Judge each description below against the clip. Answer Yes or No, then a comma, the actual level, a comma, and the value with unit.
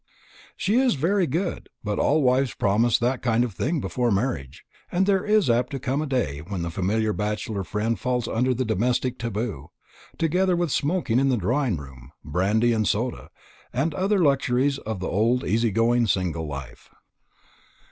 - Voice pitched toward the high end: No, low, 120 Hz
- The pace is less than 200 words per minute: Yes, average, 175 wpm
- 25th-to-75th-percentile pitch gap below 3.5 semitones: No, average, 5.1 semitones